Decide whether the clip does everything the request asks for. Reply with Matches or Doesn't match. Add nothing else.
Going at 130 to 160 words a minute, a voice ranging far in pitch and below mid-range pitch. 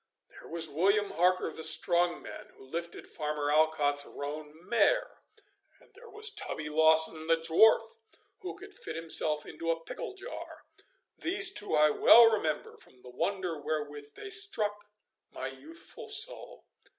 Doesn't match